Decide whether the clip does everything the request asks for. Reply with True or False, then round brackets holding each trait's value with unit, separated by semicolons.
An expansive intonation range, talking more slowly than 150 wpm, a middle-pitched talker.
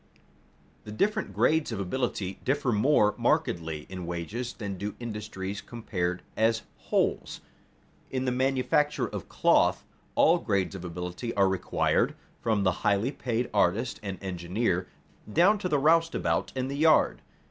False (5.9 semitones; 140 wpm; 110 Hz)